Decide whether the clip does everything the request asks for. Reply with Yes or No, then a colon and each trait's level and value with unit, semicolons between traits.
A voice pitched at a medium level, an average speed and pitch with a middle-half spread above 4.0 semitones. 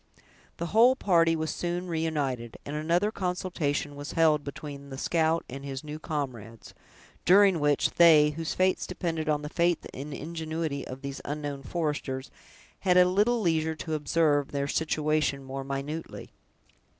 No: medium, 155 Hz; average, 150 wpm; average, 3.0 semitones